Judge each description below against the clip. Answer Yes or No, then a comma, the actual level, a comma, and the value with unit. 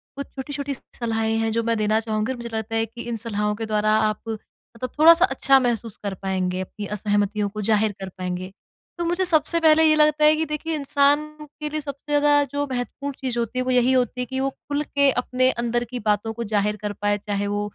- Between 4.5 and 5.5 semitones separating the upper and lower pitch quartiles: Yes, average, 5.1 semitones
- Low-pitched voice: No, high, 235 Hz